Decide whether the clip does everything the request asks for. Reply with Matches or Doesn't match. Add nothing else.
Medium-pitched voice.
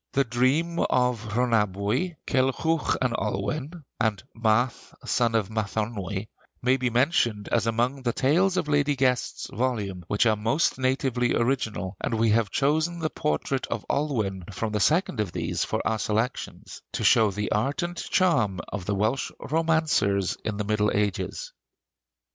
Doesn't match